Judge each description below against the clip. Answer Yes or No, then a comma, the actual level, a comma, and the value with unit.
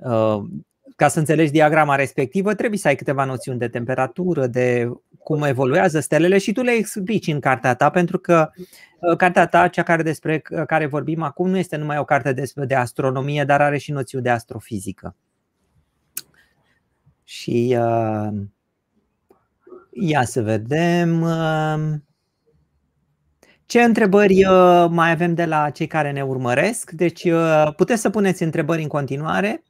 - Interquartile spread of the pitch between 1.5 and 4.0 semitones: No, average, 4.7 semitones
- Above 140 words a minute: No, average, 135 wpm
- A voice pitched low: No, medium, 155 Hz